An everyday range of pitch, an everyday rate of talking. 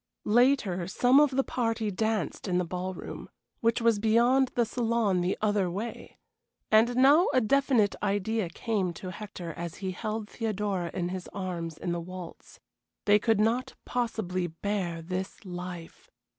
Yes: average, 4.2 semitones; average, 155 wpm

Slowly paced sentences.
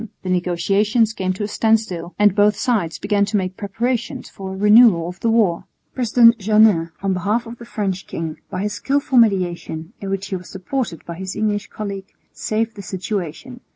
No: average, 190 wpm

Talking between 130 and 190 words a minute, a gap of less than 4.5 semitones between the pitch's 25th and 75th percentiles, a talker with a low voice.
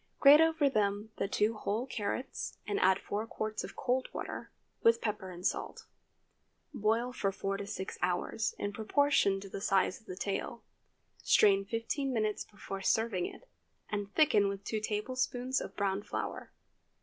No: average, 160 wpm; average, 3.2 semitones; high, 210 Hz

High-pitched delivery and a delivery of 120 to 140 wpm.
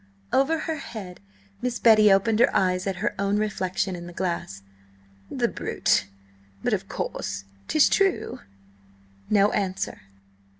Yes: high, 200 Hz; slow, 135 wpm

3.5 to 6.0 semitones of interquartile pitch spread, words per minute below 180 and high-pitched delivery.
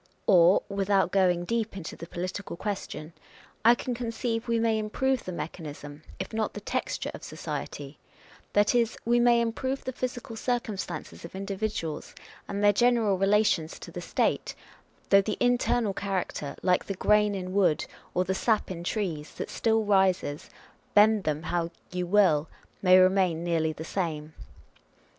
Yes: average, 4.1 semitones; average, 160 wpm; high, 195 Hz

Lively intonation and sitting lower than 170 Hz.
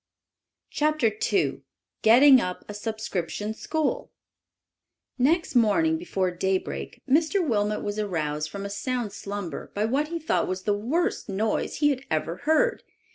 No: wide, 7.1 semitones; high, 220 Hz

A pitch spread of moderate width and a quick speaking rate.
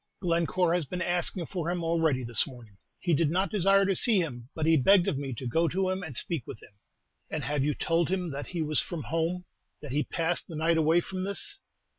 Yes: average, 3.3 semitones; fast, 235 wpm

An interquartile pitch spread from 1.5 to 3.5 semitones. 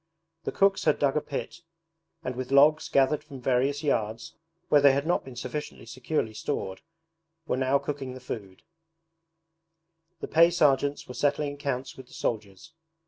Yes: average, 2.7 semitones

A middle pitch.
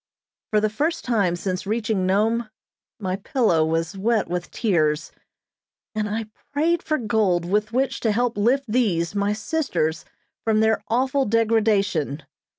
No: high, 215 Hz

